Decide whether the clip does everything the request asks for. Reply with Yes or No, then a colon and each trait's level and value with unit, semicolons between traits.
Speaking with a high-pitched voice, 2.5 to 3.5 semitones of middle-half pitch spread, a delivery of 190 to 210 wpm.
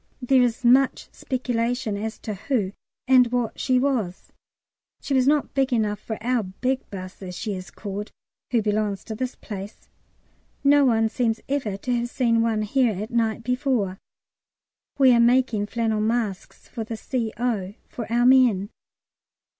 No: high, 230 Hz; average, 3.2 semitones; average, 160 wpm